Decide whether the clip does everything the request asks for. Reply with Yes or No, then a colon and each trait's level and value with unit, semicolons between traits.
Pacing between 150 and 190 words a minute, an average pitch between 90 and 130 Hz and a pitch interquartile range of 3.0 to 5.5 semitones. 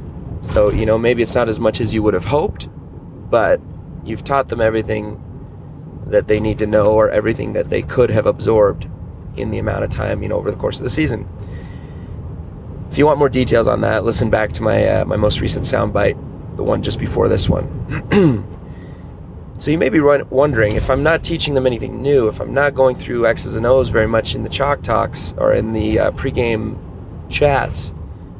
No: fast, 205 wpm; low, 115 Hz; average, 3.8 semitones